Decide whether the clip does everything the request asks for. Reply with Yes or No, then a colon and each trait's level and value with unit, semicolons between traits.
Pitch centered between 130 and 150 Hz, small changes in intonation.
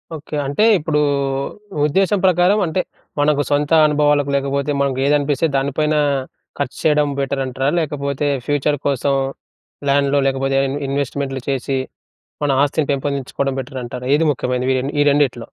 Yes: medium, 140 Hz; narrow, 1.6 semitones